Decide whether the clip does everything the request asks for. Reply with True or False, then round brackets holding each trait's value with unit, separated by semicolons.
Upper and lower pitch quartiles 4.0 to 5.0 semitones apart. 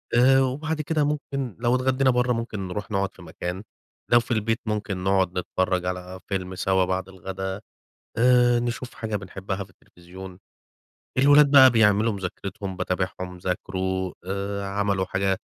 True (4.4 semitones)